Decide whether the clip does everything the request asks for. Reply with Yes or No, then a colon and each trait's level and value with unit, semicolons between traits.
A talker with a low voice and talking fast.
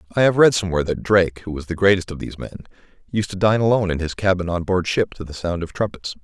Yes: very low, 95 Hz; fast, 270 wpm